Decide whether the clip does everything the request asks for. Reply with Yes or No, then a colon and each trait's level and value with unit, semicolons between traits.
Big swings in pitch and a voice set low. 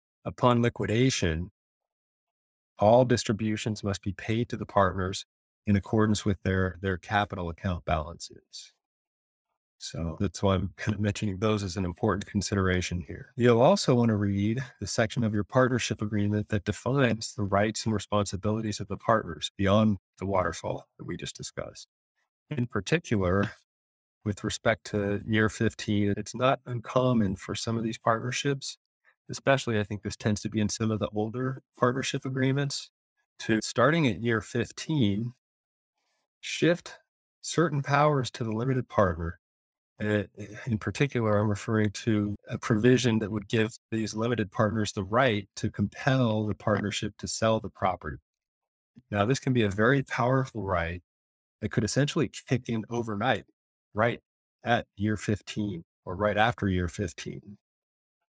No: average, 2.9 semitones; low, 105 Hz